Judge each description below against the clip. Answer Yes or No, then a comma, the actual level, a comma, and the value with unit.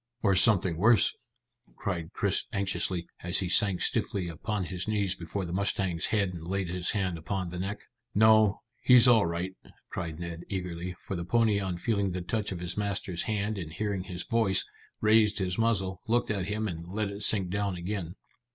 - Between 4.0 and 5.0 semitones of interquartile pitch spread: No, average, 2.8 semitones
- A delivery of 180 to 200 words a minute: Yes, average, 190 wpm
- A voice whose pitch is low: Yes, very low, 95 Hz